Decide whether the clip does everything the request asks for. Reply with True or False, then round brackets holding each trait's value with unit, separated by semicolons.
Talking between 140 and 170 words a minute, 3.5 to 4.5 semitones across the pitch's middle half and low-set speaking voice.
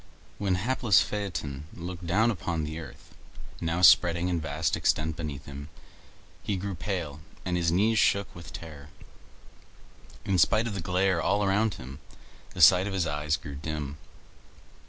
True (155 wpm; 4.0 semitones; 85 Hz)